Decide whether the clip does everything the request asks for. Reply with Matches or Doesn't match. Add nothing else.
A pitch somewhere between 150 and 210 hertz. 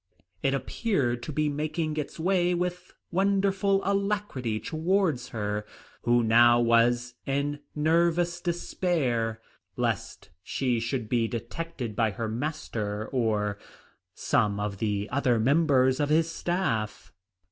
Doesn't match